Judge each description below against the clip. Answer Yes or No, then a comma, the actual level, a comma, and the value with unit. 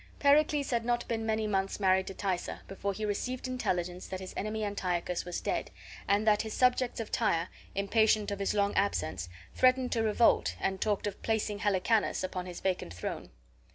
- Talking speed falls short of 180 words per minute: No, average, 185 wpm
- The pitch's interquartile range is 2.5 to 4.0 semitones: Yes, average, 3.0 semitones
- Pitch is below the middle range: No, high, 205 Hz